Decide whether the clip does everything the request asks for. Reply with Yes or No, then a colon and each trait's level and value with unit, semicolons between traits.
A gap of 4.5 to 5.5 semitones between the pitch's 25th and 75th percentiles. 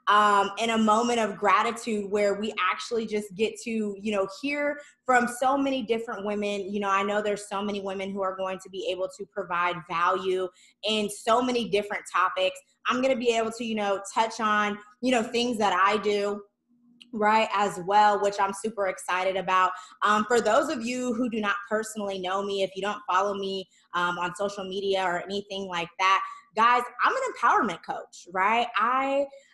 No: average, 3.1 semitones